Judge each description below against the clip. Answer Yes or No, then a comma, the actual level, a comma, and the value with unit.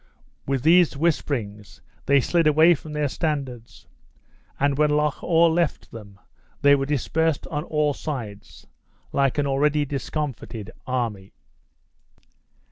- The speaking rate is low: Yes, slow, 125 wpm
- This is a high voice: No, medium, 145 Hz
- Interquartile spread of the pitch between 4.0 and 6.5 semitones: No, average, 3.3 semitones